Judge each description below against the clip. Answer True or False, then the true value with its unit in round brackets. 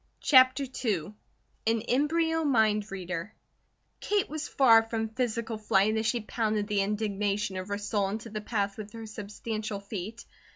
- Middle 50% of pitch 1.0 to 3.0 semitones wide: True (2.4 semitones)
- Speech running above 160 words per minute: False (155 wpm)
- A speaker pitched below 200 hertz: False (215 Hz)